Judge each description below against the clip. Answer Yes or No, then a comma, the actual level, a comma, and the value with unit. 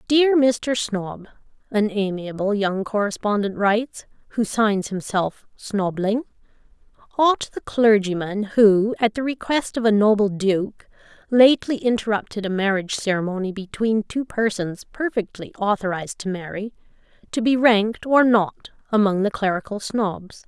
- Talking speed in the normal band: No, slow, 130 wpm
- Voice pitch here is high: Yes, high, 210 Hz